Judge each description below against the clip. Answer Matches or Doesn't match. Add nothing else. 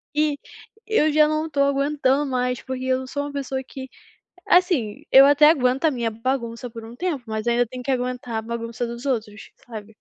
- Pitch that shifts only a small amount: Doesn't match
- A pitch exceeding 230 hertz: Matches